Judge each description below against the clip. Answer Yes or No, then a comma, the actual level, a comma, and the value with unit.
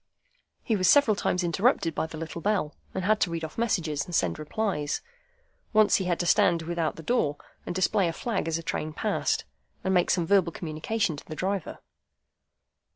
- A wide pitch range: No, average, 3.9 semitones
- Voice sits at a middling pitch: Yes, medium, 175 Hz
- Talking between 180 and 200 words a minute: Yes, average, 195 wpm